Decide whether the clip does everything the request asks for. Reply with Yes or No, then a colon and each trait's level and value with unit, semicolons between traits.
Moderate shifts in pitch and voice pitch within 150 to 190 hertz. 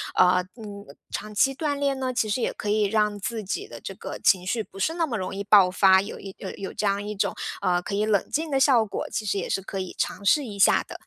No: average, 4.1 semitones; high, 210 Hz